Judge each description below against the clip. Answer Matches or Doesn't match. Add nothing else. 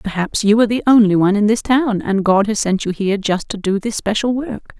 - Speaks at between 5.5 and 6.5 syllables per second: Matches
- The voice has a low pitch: Doesn't match